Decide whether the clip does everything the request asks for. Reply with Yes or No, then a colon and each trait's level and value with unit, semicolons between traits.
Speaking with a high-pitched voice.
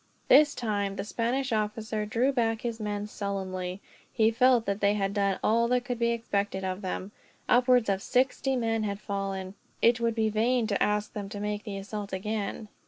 Yes: high, 215 Hz